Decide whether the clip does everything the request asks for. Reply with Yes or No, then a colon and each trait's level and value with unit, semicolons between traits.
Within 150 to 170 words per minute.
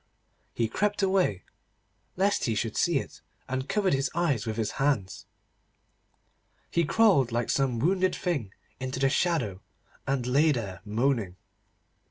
No: average, 140 wpm